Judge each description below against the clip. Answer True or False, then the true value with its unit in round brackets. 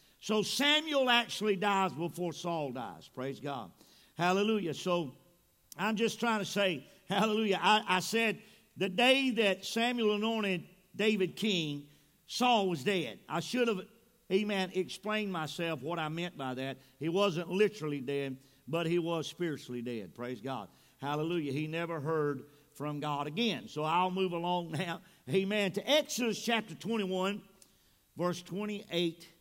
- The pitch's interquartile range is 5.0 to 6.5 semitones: True (5.5 semitones)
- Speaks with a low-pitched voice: False (180 Hz)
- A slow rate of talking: False (145 wpm)